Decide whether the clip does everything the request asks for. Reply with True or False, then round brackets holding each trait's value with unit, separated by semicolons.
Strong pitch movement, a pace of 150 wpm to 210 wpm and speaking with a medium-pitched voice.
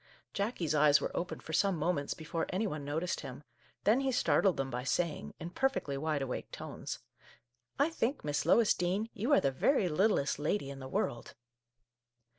True (6.4 semitones; 190 wpm; 165 Hz)